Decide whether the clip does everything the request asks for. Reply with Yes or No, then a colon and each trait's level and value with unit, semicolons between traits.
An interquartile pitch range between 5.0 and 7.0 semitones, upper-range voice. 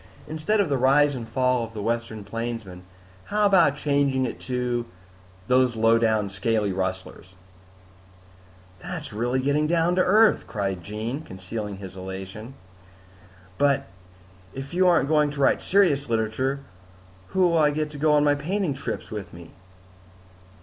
No: wide, 5.5 semitones; low, 130 Hz